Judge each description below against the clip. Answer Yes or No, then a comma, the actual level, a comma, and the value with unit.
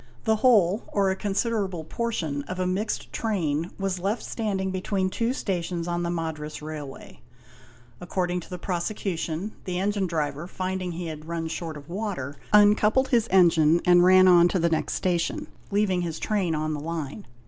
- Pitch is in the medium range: Yes, medium, 180 Hz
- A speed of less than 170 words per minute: No, average, 175 wpm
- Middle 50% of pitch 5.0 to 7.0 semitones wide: No, average, 3.3 semitones